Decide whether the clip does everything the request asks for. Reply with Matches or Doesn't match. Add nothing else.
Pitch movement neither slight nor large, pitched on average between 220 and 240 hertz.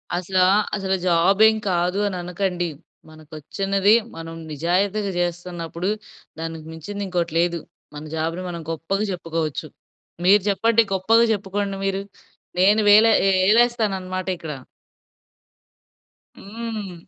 Doesn't match